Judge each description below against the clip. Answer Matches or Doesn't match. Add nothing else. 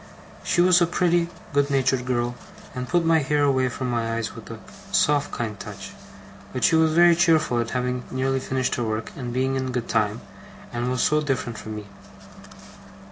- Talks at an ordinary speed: Matches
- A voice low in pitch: Matches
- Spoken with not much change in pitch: Doesn't match